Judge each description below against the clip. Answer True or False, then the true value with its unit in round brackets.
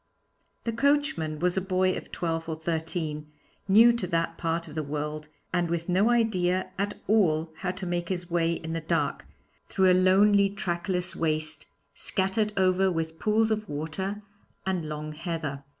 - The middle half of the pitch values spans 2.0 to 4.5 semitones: True (3.1 semitones)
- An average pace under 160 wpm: False (165 wpm)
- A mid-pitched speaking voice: True (175 Hz)